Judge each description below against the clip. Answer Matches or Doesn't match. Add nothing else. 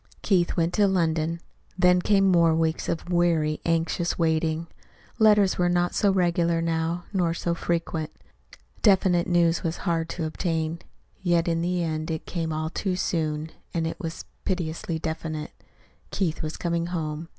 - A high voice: Doesn't match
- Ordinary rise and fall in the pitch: Doesn't match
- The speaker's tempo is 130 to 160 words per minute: Matches